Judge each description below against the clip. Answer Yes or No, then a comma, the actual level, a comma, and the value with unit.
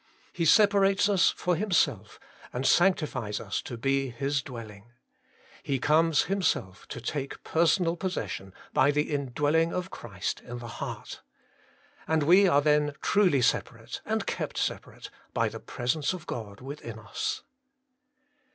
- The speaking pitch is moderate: Yes, medium, 145 Hz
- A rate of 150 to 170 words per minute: No, average, 140 wpm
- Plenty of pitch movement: Yes, wide, 5.9 semitones